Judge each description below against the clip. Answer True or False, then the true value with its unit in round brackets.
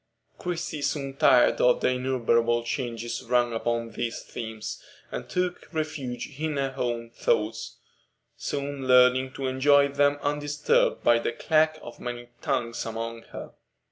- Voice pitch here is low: True (125 Hz)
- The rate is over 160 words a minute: False (140 wpm)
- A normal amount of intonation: True (3.3 semitones)